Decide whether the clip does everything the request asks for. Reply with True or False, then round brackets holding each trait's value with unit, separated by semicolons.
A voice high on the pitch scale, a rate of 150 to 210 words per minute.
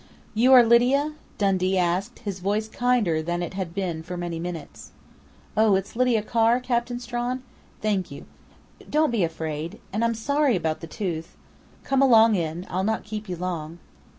True (200 Hz; 170 wpm)